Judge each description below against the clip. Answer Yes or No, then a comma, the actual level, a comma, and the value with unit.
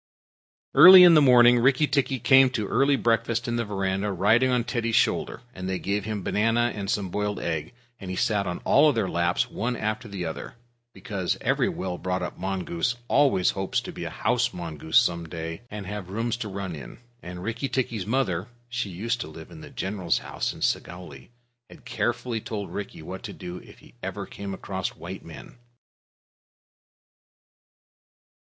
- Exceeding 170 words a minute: Yes, average, 180 wpm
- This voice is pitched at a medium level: No, low, 105 Hz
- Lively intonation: No, average, 4.6 semitones